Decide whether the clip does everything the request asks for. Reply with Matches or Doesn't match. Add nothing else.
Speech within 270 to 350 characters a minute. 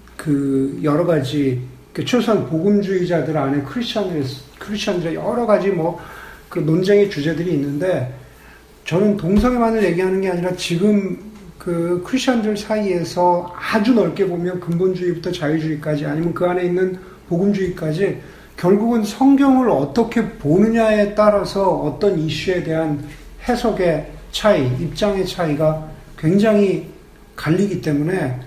Matches